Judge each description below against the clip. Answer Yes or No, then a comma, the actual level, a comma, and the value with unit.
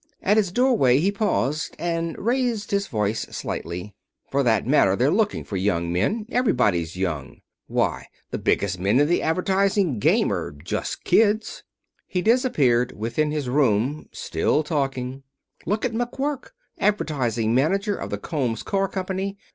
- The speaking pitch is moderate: Yes, medium, 150 Hz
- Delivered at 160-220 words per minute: No, average, 145 wpm